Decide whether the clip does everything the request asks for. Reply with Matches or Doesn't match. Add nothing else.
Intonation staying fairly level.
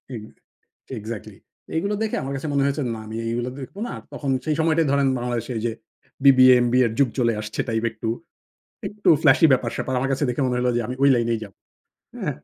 Doesn't match